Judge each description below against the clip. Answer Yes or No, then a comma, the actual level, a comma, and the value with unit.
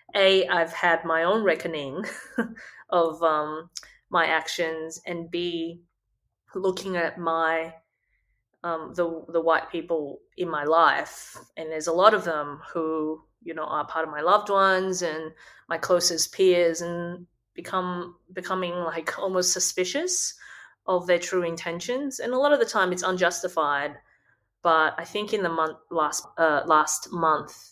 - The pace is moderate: Yes, average, 150 wpm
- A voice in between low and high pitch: Yes, medium, 170 Hz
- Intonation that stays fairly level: Yes, narrow, 2.3 semitones